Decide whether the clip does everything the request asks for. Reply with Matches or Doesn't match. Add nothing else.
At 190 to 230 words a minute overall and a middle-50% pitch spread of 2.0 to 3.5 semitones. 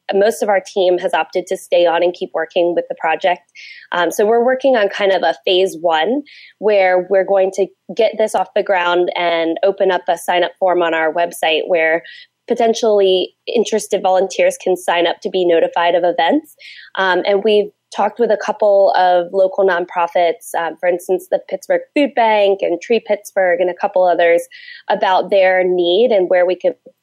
Matches